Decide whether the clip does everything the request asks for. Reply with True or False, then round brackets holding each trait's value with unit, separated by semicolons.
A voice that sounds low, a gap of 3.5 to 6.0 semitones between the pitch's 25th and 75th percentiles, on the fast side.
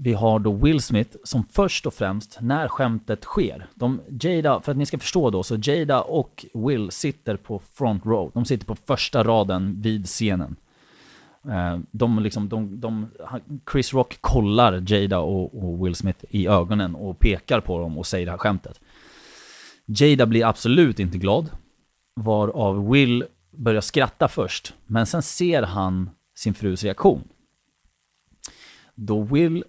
False (110 Hz; 4.0 semitones; 155 wpm)